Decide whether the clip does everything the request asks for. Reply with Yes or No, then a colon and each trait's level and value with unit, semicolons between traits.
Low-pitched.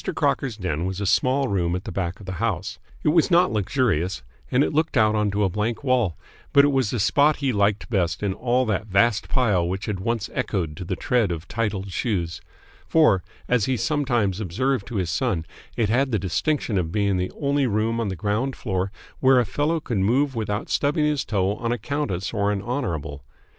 Yes: low, 105 Hz